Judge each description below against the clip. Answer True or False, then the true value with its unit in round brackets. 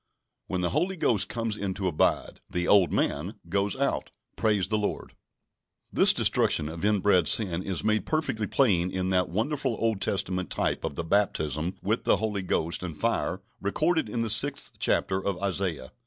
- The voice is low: True (100 Hz)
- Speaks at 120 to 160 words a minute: False (175 wpm)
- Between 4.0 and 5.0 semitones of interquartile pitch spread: False (3.4 semitones)